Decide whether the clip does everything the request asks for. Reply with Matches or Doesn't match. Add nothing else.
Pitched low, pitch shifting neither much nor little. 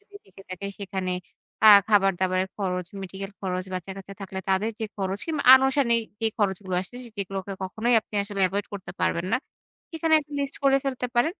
Doesn't match